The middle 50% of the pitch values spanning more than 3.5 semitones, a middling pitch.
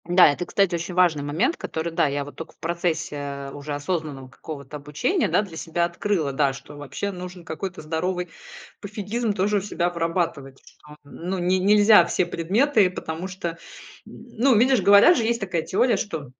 Yes: average, 4.7 semitones; medium, 175 Hz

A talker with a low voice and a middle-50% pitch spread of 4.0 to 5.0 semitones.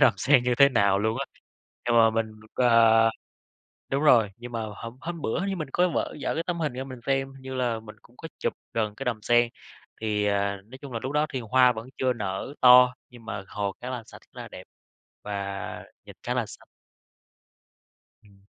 No: low, 120 Hz; average, 3.2 semitones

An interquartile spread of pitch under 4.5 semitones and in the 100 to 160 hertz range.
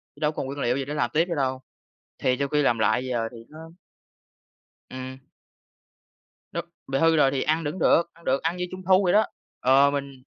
Yes: average, 3.8 semitones; medium, 140 Hz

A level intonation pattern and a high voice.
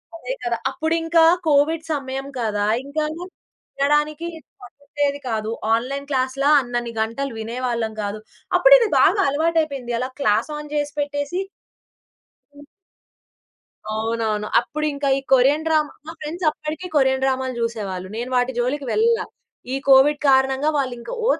No: average, 3.7 semitones; very high, 275 Hz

